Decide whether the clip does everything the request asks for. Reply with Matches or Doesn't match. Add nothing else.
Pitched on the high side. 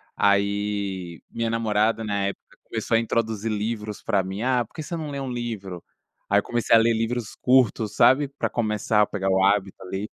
Doesn't match